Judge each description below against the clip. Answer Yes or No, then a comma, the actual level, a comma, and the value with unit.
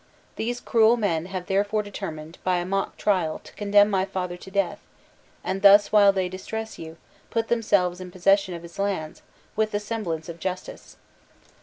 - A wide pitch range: No, narrow, 2.5 semitones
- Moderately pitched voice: No, high, 195 Hz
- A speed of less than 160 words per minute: No, average, 175 wpm